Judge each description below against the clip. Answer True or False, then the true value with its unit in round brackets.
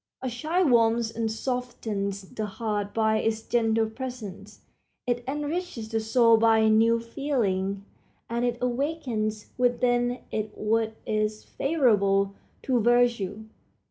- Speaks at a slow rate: True (120 wpm)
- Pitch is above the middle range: True (225 Hz)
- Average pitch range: False (2.3 semitones)